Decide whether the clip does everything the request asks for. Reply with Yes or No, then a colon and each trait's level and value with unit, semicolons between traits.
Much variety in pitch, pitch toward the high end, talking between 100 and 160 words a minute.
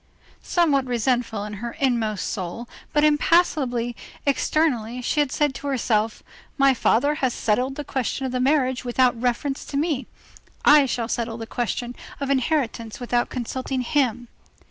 No: average, 2.9 semitones; very high, 255 Hz; average, 155 wpm